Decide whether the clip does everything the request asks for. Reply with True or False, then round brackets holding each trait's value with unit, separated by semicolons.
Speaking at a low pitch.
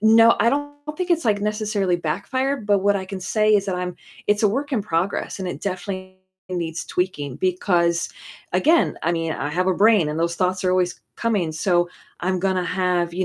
False (185 Hz)